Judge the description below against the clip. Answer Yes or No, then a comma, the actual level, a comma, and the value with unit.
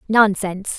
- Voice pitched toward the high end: Yes, high, 200 Hz